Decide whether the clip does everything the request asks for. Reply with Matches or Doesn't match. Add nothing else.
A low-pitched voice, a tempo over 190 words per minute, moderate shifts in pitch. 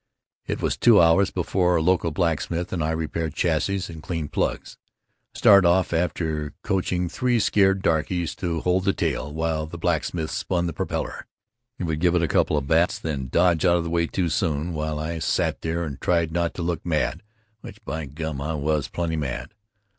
Doesn't match